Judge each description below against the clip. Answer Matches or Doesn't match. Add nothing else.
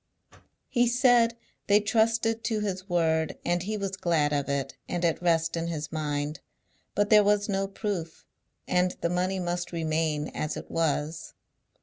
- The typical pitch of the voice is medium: Matches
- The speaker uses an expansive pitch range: Doesn't match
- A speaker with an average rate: Matches